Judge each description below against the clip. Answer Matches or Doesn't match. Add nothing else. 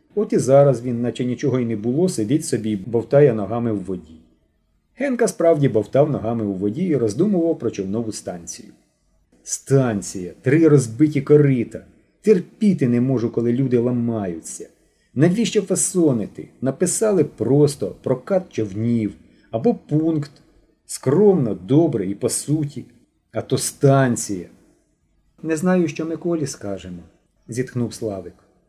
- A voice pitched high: Doesn't match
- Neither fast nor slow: Matches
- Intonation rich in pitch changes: Matches